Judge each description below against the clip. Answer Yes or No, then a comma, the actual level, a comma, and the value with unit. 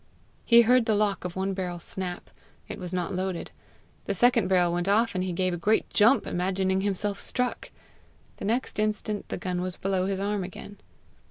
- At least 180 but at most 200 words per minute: Yes, average, 190 wpm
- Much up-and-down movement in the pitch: No, narrow, 2.5 semitones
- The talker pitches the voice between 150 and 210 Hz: Yes, high, 190 Hz